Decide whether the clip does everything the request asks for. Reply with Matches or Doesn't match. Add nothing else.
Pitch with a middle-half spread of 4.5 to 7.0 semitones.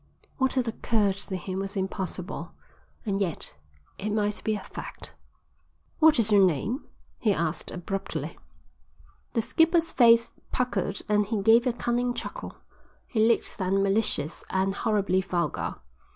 Doesn't match